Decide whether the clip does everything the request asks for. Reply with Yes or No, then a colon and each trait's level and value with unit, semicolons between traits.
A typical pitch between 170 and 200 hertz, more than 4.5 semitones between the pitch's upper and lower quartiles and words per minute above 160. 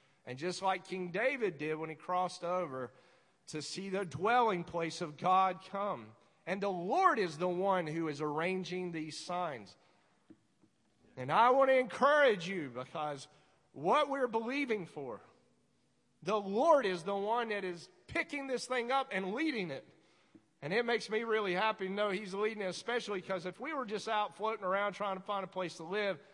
No: high, 190 Hz; average, 3.7 semitones; average, 185 wpm